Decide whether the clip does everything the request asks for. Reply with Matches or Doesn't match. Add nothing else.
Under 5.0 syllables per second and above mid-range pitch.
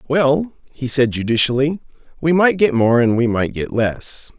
Doesn't match